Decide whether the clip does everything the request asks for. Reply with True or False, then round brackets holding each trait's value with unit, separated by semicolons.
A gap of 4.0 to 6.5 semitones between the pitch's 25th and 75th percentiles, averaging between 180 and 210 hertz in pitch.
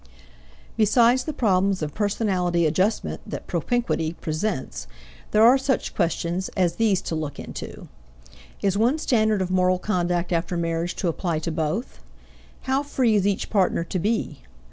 True (4.5 semitones; 190 Hz)